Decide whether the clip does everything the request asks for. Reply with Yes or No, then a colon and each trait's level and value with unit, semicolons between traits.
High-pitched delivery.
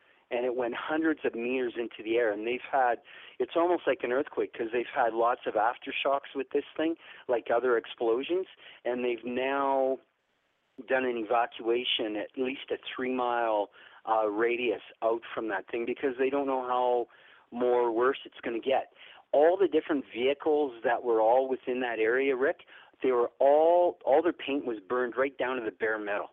No: low, 130 Hz